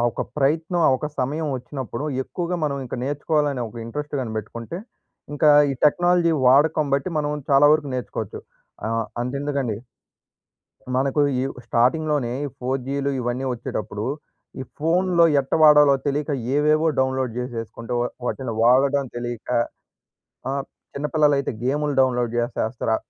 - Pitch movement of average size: Yes, average, 3.4 semitones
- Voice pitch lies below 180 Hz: Yes, medium, 140 Hz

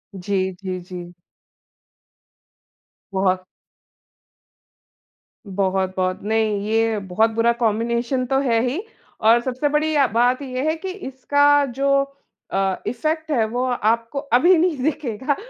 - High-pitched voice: Yes, high, 235 Hz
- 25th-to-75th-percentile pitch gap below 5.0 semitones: No, average, 5.3 semitones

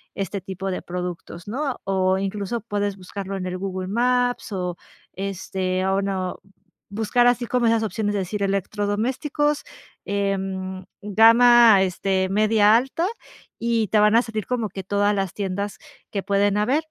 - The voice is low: No, high, 200 Hz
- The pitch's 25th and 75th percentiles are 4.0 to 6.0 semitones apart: No, average, 2.9 semitones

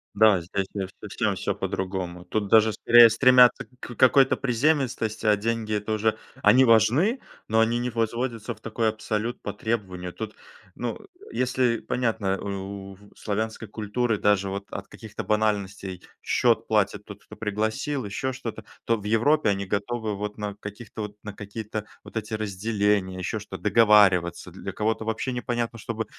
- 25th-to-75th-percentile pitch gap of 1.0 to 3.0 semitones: Yes, narrow, 2.4 semitones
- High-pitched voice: No, low, 110 Hz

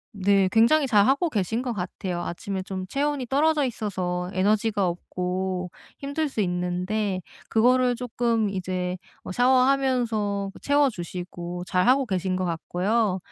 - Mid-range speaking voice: No, high, 205 Hz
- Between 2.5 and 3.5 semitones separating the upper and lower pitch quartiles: No, wide, 5.4 semitones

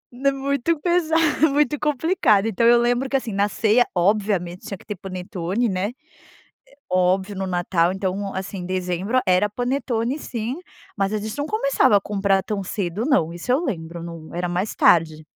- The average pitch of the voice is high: Yes, high, 205 Hz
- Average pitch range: No, wide, 5.9 semitones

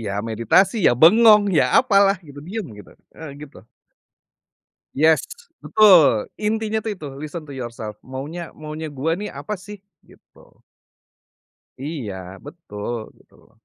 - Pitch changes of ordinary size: No, wide, 7.0 semitones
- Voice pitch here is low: No, medium, 160 Hz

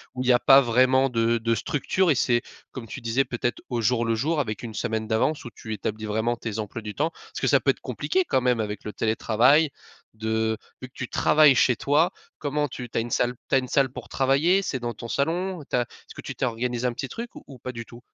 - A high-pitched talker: No, low, 125 Hz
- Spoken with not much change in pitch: No, average, 3.2 semitones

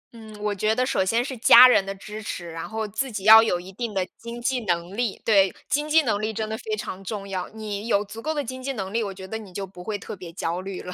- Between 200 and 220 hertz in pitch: Yes, high, 210 Hz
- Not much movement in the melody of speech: No, average, 3.2 semitones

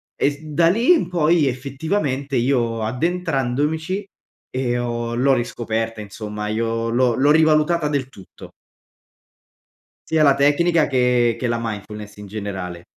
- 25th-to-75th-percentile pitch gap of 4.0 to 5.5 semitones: Yes, average, 5.0 semitones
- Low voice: Yes, low, 130 Hz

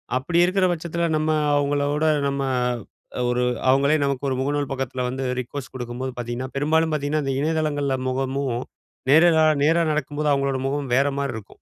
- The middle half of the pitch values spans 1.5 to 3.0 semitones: Yes, narrow, 2.6 semitones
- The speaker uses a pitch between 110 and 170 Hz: Yes, medium, 140 Hz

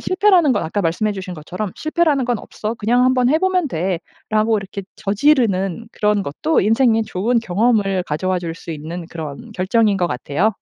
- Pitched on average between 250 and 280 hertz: No, high, 210 Hz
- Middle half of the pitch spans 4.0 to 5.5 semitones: Yes, average, 5.1 semitones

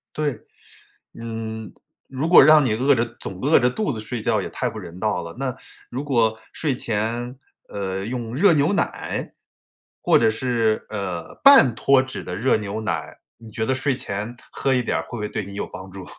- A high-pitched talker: No, low, 115 Hz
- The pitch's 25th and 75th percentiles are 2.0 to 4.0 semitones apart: Yes, average, 3.7 semitones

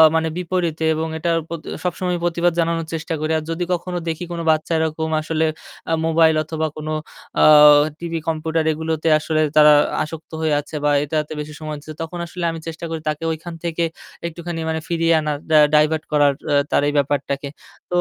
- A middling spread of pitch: No, narrow, 1.4 semitones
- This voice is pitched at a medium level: Yes, medium, 160 Hz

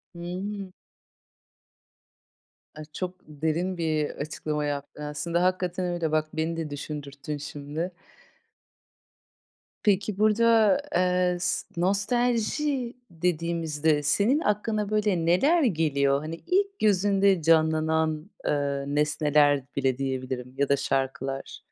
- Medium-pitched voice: Yes, medium, 165 Hz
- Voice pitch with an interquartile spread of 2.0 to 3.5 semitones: No, average, 5.0 semitones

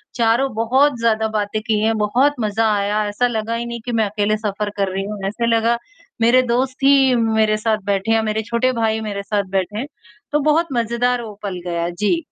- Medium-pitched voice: No, high, 220 Hz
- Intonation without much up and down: Yes, narrow, 2.2 semitones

